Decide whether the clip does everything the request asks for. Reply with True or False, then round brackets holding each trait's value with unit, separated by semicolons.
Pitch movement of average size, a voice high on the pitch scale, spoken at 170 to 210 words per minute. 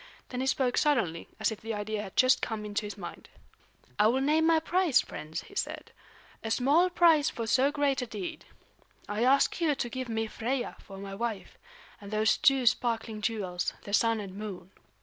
True (4.5 semitones; 230 Hz; 195 wpm)